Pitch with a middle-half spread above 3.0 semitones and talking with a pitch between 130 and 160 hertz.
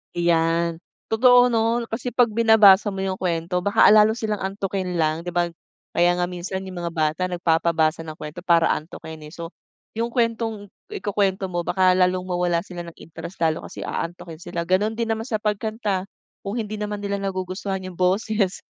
No: average, 3.6 semitones; medium, 185 Hz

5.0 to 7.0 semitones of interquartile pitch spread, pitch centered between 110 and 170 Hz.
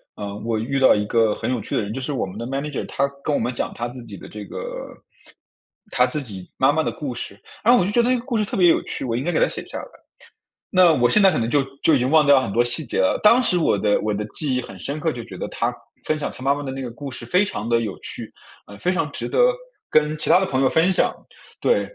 Yes: wide, 5.4 semitones; low, 135 Hz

